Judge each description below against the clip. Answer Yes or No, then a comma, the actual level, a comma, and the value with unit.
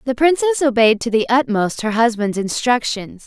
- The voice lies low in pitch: No, high, 240 Hz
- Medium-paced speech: Yes, average, 165 wpm